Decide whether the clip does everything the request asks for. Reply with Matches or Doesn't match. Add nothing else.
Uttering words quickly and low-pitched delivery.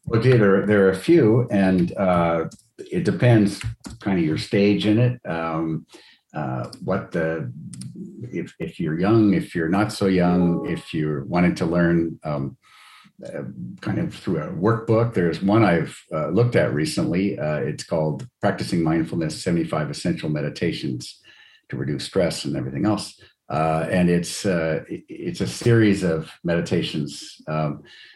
Doesn't match